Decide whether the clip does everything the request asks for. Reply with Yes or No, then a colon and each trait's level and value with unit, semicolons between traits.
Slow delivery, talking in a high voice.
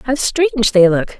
No: average, 200 wpm; high, 235 Hz